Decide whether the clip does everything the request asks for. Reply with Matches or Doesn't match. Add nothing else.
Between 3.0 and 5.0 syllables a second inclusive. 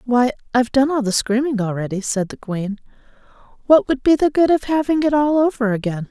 Doesn't match